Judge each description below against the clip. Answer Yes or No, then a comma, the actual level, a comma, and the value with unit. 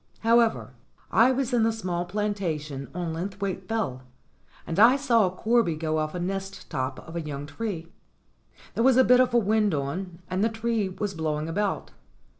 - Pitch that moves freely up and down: Yes, wide, 5.7 semitones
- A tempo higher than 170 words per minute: Yes, average, 190 wpm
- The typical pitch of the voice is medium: No, high, 195 Hz